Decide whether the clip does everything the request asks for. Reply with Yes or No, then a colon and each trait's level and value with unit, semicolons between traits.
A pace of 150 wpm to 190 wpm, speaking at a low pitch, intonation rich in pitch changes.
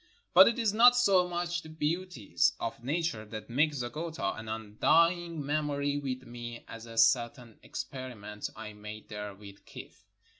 Yes: average, 160 wpm; low, 130 Hz; wide, 6.9 semitones